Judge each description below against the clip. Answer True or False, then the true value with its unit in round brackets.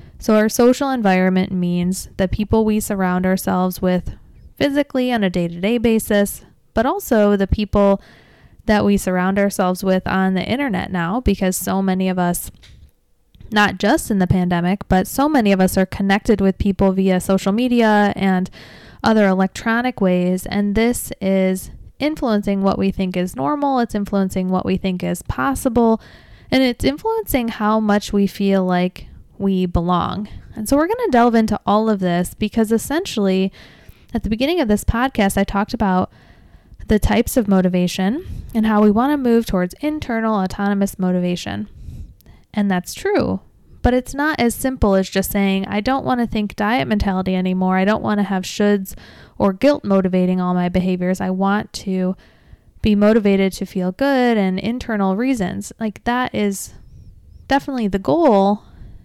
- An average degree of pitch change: True (3.4 semitones)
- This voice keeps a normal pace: True (170 wpm)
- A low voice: False (200 Hz)